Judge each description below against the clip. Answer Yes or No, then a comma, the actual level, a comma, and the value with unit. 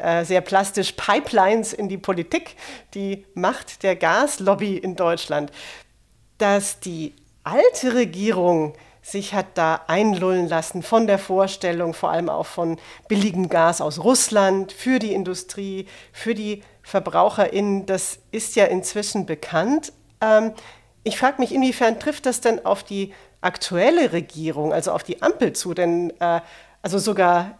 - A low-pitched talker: No, high, 195 Hz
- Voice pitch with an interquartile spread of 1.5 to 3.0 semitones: No, average, 3.7 semitones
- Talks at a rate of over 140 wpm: No, average, 135 wpm